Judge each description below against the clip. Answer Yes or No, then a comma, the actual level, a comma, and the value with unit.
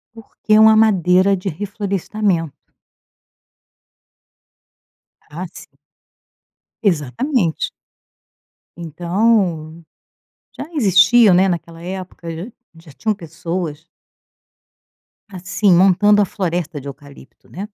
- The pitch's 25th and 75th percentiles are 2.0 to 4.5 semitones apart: Yes, average, 3.6 semitones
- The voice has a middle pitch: Yes, medium, 180 Hz